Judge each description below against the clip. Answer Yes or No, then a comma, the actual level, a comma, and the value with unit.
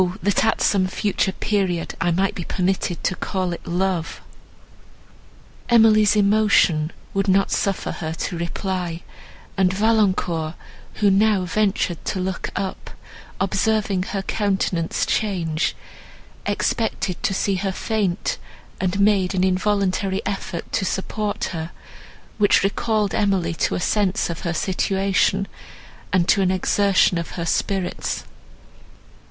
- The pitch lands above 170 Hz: Yes, high, 190 Hz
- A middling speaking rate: No, slow, 125 wpm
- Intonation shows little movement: Yes, narrow, 2.2 semitones